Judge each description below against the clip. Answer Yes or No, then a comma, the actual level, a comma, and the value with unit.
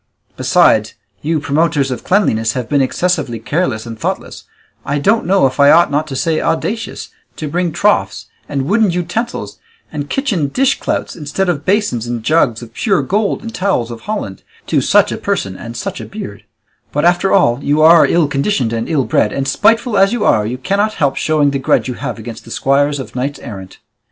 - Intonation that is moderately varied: No, wide, 6.8 semitones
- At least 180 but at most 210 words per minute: Yes, average, 195 wpm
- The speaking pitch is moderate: Yes, medium, 145 Hz